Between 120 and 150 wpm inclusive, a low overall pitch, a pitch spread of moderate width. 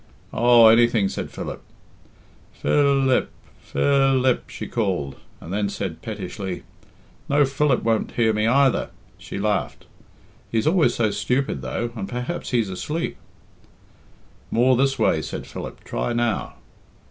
Yes: slow, 135 wpm; low, 120 Hz; average, 4.5 semitones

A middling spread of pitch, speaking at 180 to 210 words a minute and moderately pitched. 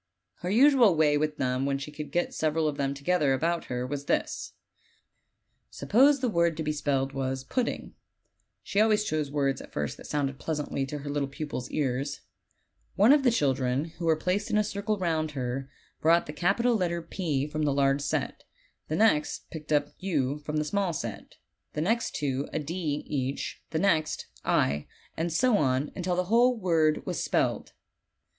Yes: average, 4.6 semitones; average, 185 wpm; medium, 155 Hz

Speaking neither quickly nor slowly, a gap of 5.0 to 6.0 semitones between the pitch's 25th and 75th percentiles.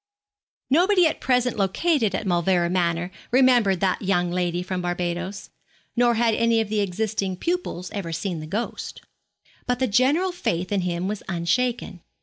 Yes: average, 155 wpm; wide, 5.5 semitones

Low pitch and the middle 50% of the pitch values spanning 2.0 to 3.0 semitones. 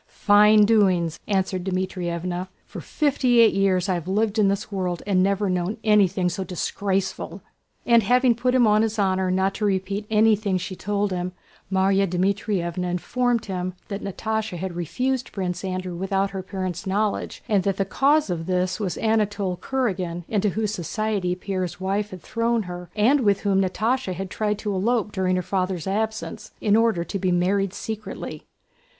No: high, 195 Hz; narrow, 2.6 semitones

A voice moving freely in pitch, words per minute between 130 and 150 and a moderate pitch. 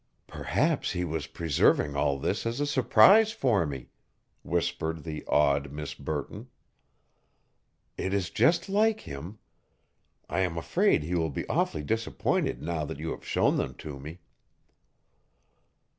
No: wide, 6.7 semitones; average, 140 wpm; very low, 80 Hz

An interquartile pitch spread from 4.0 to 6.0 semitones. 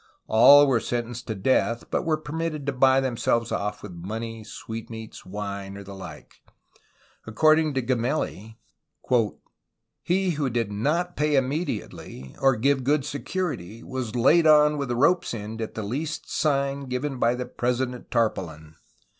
Yes: average, 4.6 semitones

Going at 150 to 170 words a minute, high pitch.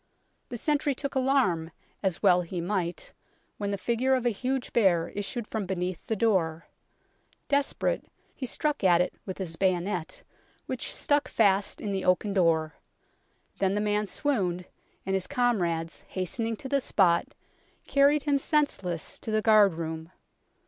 Yes: average, 155 wpm; high, 200 Hz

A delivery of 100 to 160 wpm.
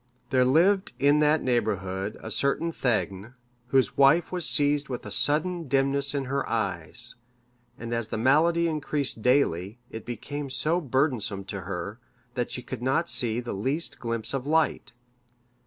Yes: average, 155 wpm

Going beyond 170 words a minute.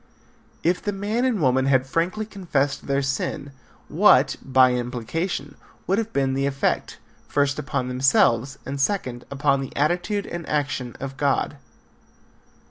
No: average, 140 wpm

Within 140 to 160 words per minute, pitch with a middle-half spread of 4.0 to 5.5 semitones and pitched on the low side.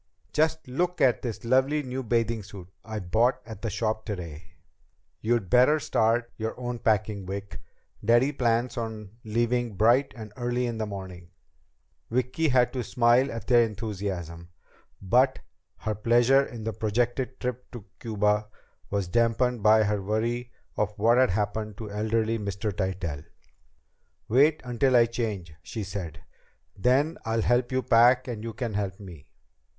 No: average, 155 wpm; average, 2.9 semitones; low, 115 Hz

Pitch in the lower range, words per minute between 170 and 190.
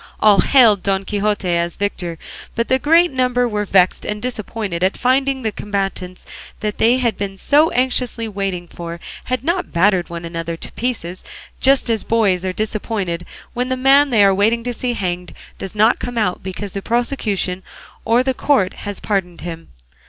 No: high, 210 Hz; average, 180 wpm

